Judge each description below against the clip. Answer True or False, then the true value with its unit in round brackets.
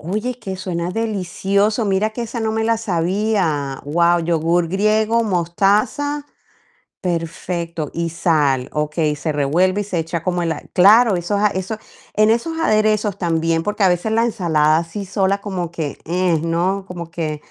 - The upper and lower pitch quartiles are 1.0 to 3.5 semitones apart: False (4.3 semitones)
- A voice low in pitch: False (185 Hz)